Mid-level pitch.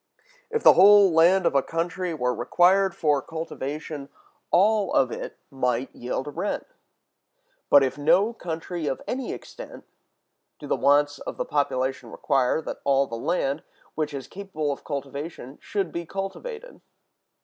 Yes: medium, 155 Hz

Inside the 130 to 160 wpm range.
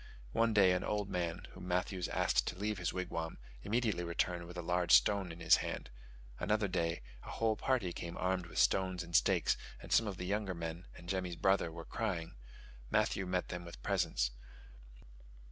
No: average, 185 wpm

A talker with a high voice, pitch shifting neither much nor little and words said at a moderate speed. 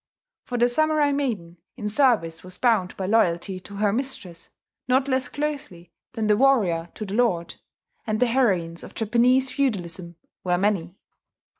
No: high, 215 Hz; wide, 6.2 semitones; average, 155 wpm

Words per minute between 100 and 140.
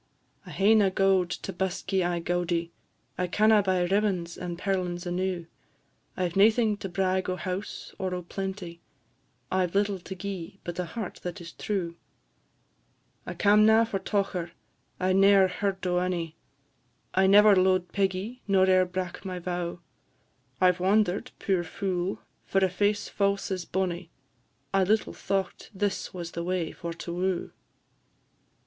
No: average, 160 wpm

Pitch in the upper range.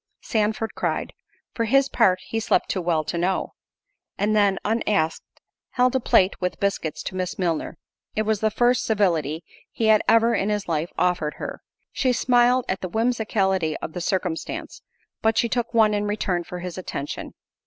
Yes: high, 205 Hz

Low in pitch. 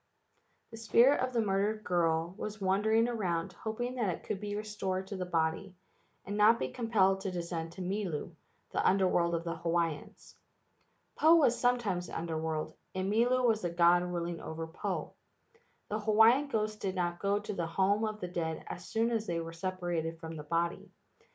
No: high, 190 Hz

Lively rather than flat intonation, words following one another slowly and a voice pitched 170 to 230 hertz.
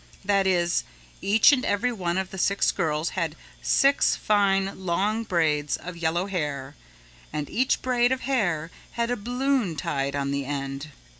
No: wide, 6.5 semitones; average, 160 wpm; medium, 185 Hz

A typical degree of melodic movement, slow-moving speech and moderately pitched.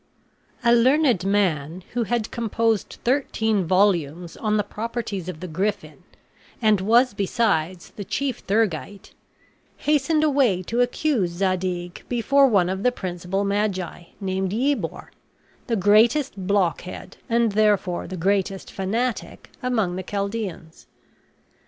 No: average, 4.1 semitones; slow, 120 wpm; high, 205 Hz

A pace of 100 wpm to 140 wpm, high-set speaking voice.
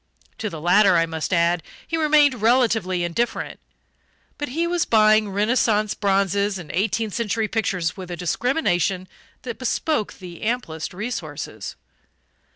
Yes: slow, 135 wpm; high, 210 Hz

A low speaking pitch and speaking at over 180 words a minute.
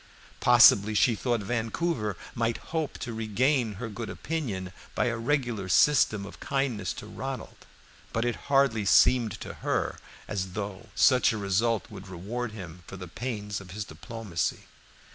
No: low, 110 Hz; average, 155 wpm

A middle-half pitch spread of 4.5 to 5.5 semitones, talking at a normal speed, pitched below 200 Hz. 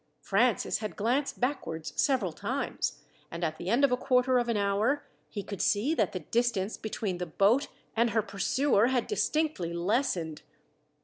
No: average, 5.0 semitones; average, 170 wpm; high, 220 Hz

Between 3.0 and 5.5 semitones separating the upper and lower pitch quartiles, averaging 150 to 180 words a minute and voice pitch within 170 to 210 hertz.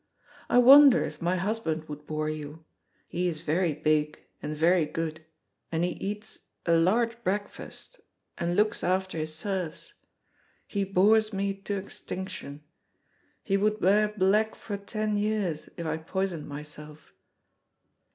No: average, 4.9 semitones; average, 140 wpm; medium, 185 Hz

